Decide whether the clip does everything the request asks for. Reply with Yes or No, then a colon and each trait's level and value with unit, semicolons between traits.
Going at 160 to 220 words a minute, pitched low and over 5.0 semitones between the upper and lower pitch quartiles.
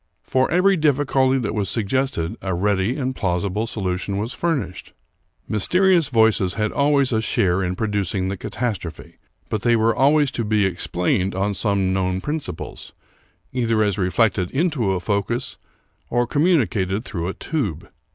No: average, 150 wpm; low, 110 Hz; wide, 5.5 semitones